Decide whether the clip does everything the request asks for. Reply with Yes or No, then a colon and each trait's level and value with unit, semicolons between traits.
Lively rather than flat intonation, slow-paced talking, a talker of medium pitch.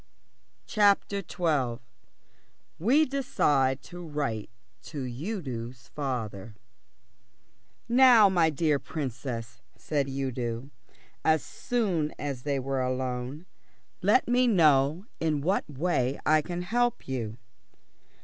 Yes: wide, 5.9 semitones; slow, 100 wpm; medium, 145 Hz